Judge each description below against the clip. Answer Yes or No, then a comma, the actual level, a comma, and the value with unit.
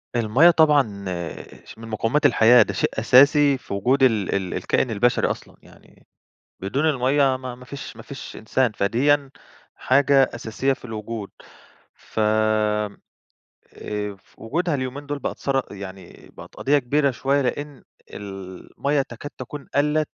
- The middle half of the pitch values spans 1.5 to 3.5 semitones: No, average, 4.7 semitones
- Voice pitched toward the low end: Yes, low, 130 Hz